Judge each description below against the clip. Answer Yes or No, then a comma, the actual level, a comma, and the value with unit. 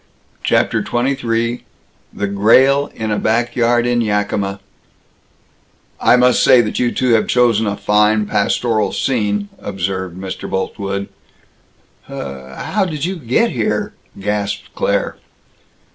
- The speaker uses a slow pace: Yes, slow, 120 wpm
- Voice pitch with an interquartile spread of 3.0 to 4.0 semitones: Yes, average, 3.3 semitones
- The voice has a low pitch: Yes, low, 110 Hz